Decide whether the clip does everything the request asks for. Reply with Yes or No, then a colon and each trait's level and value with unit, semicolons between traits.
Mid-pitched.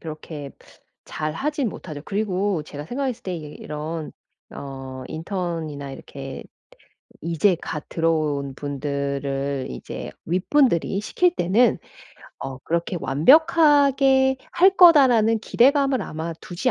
Yes: medium, 170 Hz